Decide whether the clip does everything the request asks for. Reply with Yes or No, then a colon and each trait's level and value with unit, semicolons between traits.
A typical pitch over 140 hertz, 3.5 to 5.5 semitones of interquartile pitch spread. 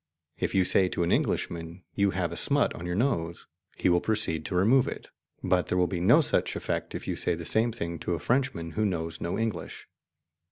No: very low, 90 Hz; average, 4.4 semitones